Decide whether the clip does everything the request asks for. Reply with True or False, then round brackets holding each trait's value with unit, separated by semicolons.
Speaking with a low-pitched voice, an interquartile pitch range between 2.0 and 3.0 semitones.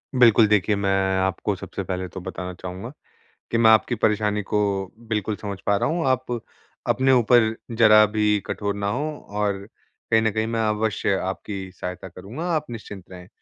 True (105 Hz; 2.6 semitones)